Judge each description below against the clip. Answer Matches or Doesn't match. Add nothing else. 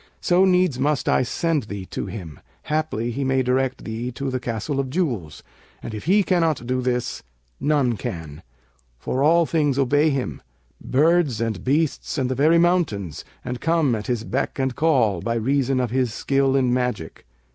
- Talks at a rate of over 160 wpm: Matches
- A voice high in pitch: Doesn't match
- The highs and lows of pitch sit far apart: Doesn't match